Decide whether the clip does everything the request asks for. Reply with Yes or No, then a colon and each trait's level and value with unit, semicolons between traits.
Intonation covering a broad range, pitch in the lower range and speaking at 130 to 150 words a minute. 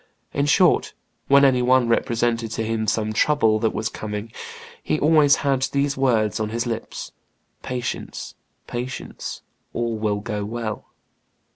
No: average, 3.5 semitones; low, 115 Hz; average, 140 wpm